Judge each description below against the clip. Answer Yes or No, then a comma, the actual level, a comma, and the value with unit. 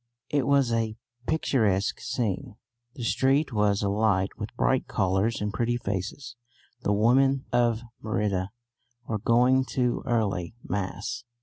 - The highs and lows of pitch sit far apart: No, average, 3.6 semitones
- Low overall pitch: Yes, low, 115 Hz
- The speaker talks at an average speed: No, slow, 125 wpm